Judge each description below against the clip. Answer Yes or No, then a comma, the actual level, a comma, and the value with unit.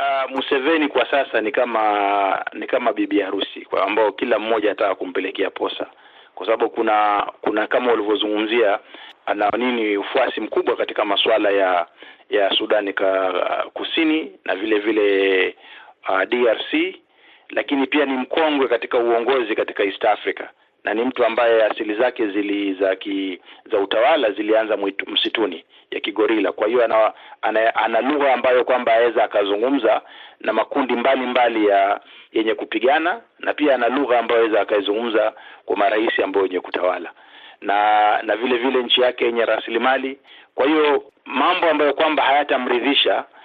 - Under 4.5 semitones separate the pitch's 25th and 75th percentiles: No, average, 5.3 semitones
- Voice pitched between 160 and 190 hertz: No, low, 120 Hz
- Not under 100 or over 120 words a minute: No, fast, 140 wpm